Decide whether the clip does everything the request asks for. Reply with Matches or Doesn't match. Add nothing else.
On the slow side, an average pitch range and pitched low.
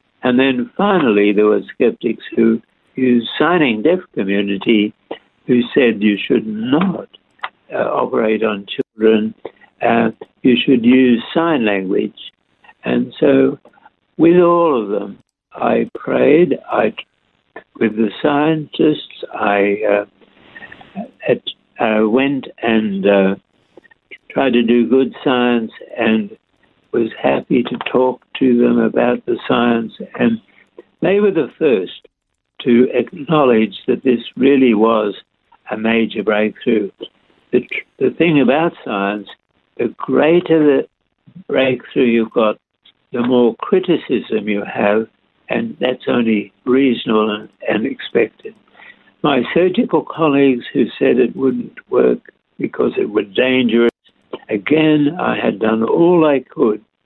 Matches